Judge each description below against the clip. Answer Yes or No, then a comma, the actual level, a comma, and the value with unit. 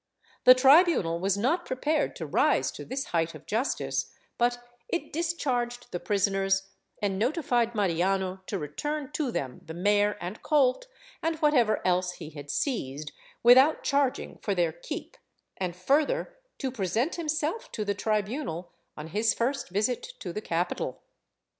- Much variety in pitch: Yes, wide, 7.2 semitones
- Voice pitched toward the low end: No, high, 220 Hz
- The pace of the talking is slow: No, average, 150 wpm